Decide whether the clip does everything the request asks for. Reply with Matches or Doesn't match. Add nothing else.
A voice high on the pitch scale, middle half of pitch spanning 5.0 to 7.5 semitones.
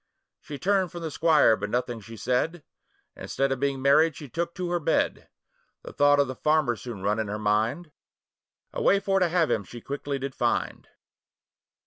Doesn't match